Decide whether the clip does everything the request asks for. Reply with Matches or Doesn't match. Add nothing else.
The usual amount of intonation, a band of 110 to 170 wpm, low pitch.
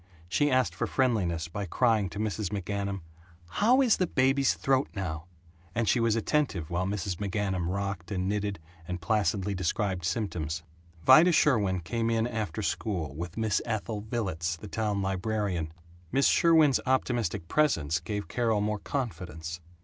Matches